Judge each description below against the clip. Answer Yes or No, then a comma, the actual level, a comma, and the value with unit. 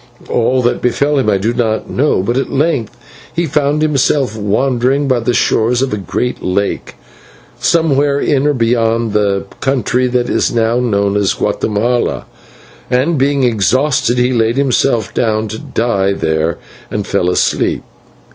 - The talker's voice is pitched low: Yes, low, 120 Hz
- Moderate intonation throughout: Yes, average, 3.9 semitones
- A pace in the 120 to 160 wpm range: Yes, average, 155 wpm